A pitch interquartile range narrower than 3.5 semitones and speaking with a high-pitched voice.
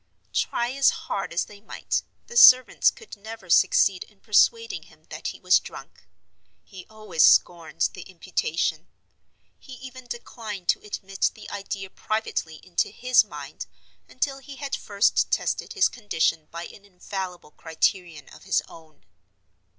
No: average, 5.2 semitones; high, 200 Hz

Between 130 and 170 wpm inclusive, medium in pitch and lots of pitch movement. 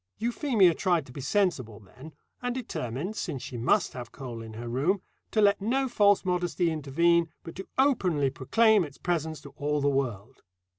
No: average, 180 wpm; medium, 160 Hz; wide, 7.2 semitones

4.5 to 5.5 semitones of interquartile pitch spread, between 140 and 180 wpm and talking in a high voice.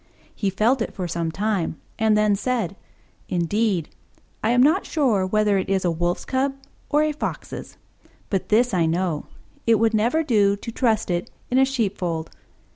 Yes: average, 4.8 semitones; average, 175 wpm; high, 210 Hz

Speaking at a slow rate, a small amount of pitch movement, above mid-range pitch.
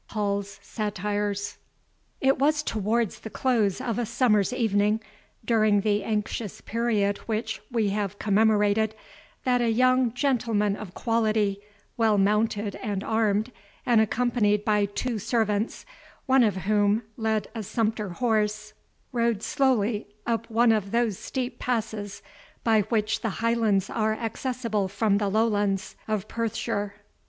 Yes: slow, 130 wpm; narrow, 2.1 semitones; high, 215 Hz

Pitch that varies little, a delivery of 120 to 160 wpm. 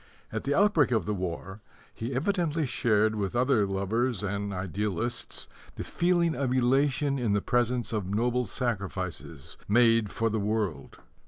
No: average, 4.1 semitones; average, 150 wpm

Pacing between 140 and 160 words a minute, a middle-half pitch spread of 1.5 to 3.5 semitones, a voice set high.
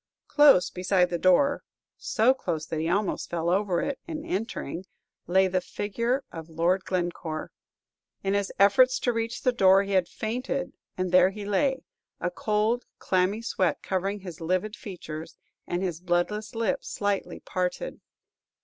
No: average, 155 wpm; average, 4.1 semitones; high, 195 Hz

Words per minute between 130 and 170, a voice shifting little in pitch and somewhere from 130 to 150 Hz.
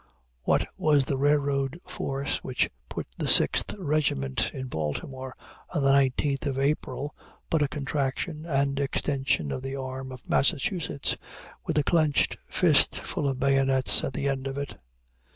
Yes: average, 150 wpm; narrow, 1.5 semitones; low, 135 Hz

